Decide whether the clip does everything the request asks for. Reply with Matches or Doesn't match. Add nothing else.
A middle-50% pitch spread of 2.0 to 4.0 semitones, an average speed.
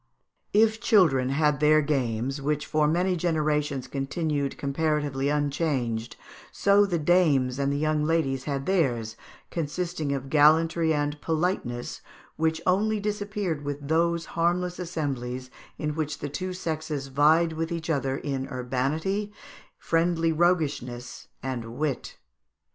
Doesn't match